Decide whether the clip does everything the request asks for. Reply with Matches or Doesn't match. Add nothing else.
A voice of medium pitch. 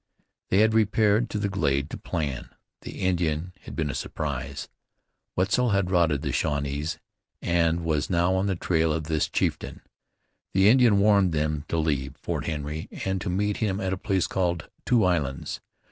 Doesn't match